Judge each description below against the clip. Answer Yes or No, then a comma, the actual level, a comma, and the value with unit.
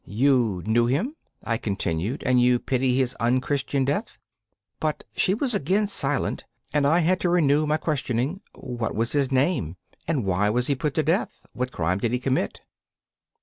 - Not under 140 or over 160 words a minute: No, average, 175 wpm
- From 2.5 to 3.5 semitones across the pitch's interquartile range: No, average, 4.3 semitones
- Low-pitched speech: Yes, low, 130 Hz